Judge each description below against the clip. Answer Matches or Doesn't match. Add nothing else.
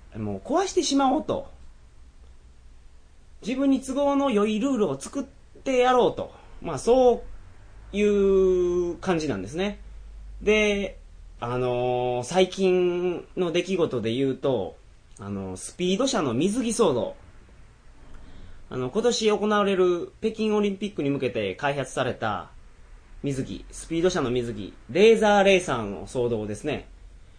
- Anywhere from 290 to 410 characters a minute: Doesn't match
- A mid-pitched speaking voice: Matches